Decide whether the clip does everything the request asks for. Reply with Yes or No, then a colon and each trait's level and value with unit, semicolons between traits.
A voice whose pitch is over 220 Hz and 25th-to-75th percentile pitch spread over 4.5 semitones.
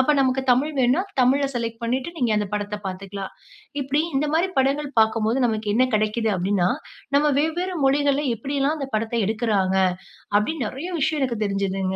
Yes: high, 245 Hz; average, 5.1 semitones